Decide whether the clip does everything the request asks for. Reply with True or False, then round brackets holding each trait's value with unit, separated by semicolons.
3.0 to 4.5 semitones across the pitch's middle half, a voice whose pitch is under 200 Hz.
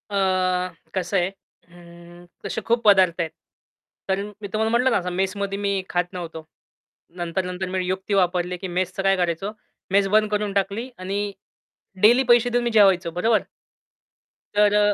False (2.5 semitones; 190 Hz)